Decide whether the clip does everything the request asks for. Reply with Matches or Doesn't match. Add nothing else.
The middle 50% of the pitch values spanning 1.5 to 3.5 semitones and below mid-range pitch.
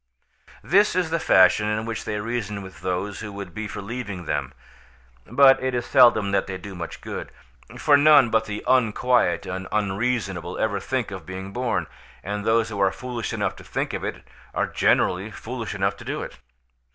Doesn't match